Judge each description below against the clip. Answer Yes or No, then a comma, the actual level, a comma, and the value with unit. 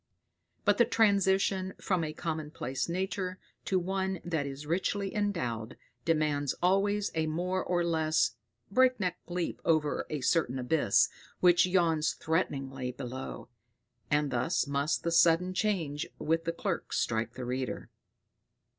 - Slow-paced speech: Yes, slow, 130 wpm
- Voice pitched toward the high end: No, medium, 165 Hz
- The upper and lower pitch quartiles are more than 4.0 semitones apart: Yes, average, 4.6 semitones